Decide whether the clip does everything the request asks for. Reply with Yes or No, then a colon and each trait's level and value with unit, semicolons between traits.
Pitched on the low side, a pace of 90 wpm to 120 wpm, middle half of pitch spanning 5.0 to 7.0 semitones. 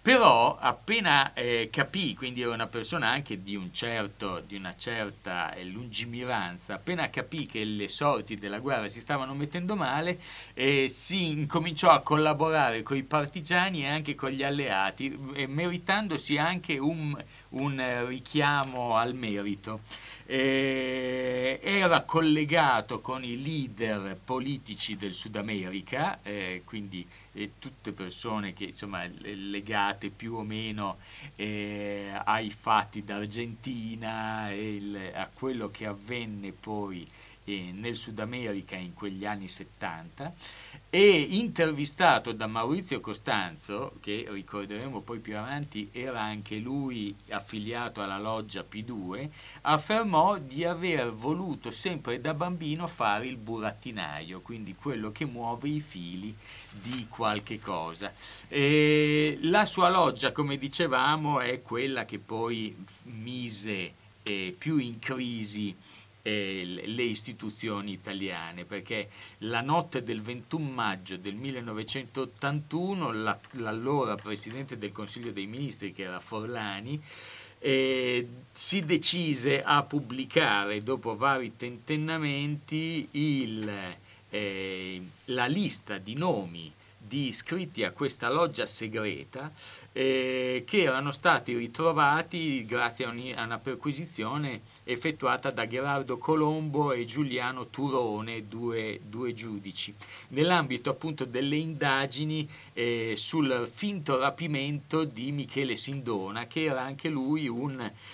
Yes: low, 120 Hz; slow, 115 wpm; wide, 5.4 semitones